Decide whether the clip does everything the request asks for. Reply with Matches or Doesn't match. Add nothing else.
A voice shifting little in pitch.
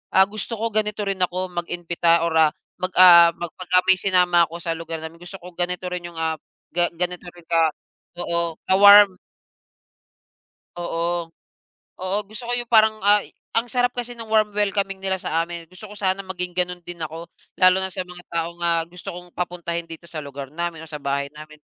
Matches